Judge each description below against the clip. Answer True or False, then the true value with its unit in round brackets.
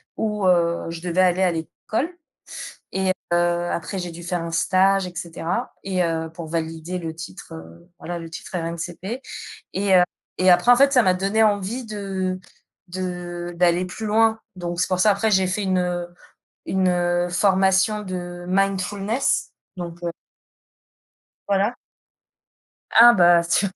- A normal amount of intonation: False (2.2 semitones)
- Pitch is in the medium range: True (180 Hz)